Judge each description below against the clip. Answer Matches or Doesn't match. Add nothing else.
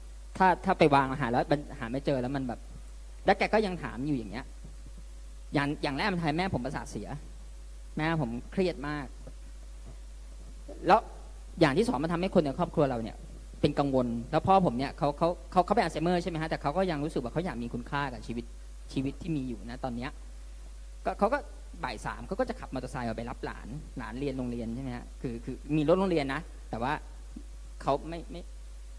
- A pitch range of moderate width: Doesn't match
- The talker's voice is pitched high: Doesn't match